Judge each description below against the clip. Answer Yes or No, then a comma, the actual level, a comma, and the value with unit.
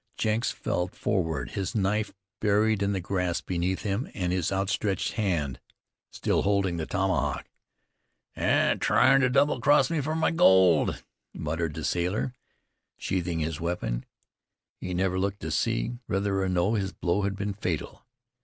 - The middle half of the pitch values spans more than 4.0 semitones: No, average, 2.9 semitones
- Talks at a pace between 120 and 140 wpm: No, average, 150 wpm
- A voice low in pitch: Yes, very low, 95 Hz